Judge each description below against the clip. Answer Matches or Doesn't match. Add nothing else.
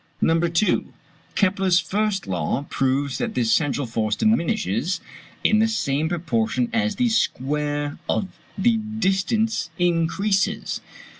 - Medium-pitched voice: Matches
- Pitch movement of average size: Doesn't match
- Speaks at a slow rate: Matches